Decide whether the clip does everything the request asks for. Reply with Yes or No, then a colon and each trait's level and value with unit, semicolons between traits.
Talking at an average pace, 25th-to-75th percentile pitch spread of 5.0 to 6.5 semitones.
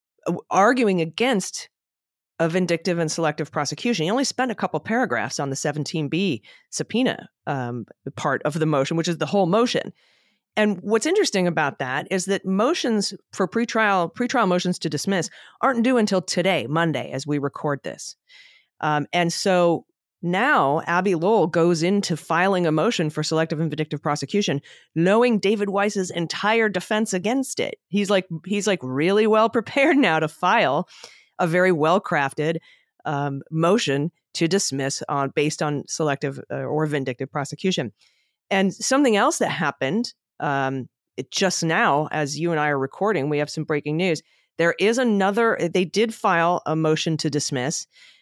Yes: average, 160 wpm; average, 5.3 semitones